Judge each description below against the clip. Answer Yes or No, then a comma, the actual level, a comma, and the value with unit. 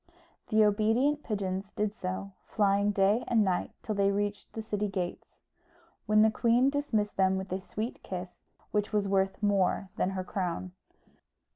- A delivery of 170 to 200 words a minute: No, average, 160 wpm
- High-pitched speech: Yes, high, 205 Hz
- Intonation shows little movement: Yes, narrow, 2.0 semitones